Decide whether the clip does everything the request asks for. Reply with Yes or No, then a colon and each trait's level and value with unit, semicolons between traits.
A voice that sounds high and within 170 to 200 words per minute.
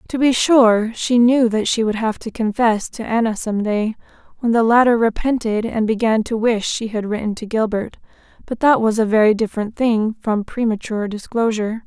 Yes: high, 225 Hz; average, 190 wpm